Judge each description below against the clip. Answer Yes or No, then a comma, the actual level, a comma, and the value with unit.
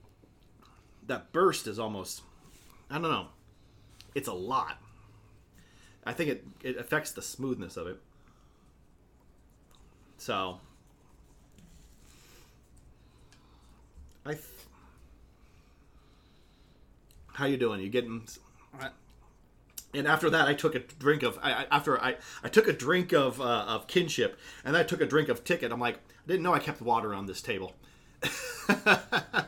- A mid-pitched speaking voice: No, low, 110 Hz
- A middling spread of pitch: No, wide, 8.7 semitones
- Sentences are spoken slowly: Yes, slow, 130 wpm